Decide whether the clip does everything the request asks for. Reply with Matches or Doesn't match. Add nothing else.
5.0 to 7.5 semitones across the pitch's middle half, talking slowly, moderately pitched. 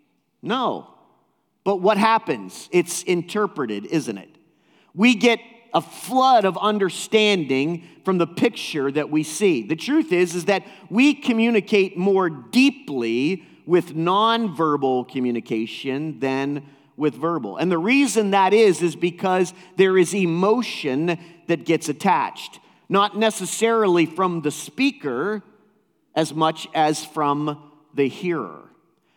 Matches